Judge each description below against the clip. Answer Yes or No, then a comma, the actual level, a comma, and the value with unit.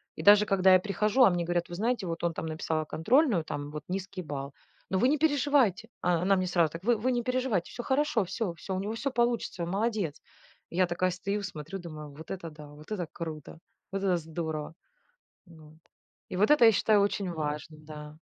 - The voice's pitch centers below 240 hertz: Yes, medium, 185 Hz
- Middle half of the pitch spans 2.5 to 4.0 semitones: No, average, 5.1 semitones